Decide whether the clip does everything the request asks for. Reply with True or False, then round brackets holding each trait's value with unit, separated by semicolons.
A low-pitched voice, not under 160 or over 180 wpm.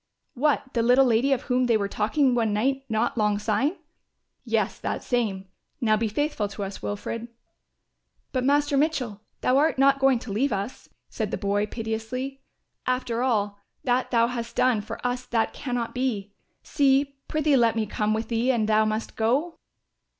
False (235 Hz; 175 wpm)